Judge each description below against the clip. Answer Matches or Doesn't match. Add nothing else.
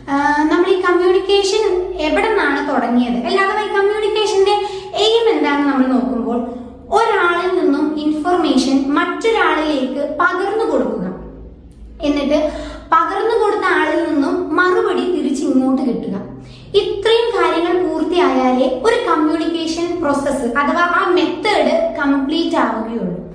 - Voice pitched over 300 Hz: Matches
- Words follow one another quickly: Doesn't match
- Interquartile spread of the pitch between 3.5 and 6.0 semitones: Matches